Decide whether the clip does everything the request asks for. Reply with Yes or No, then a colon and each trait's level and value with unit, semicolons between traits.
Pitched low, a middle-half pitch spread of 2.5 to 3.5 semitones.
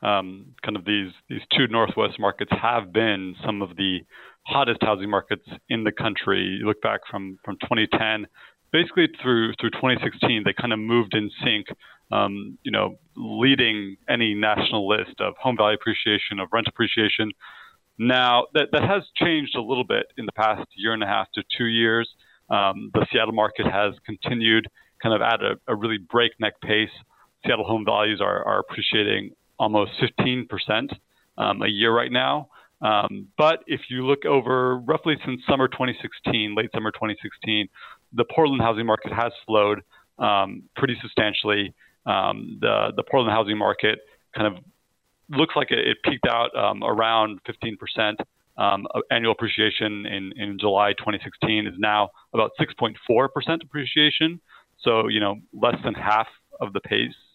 Yes: low, 110 Hz; average, 2.9 semitones